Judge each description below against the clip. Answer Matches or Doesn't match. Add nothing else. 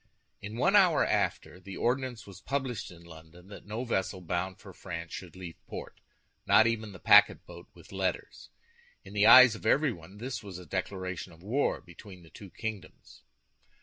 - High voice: Doesn't match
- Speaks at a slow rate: Doesn't match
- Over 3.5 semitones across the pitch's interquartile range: Matches